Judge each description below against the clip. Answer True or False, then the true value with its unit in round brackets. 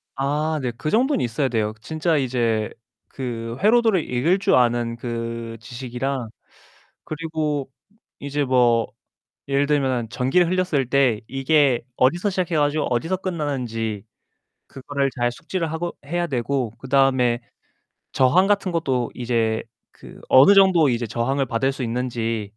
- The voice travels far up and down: False (4.7 semitones)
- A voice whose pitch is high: False (135 Hz)